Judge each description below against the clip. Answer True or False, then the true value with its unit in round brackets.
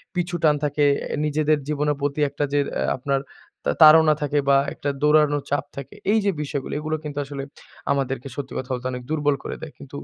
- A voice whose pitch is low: False (145 Hz)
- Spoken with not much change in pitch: True (1.7 semitones)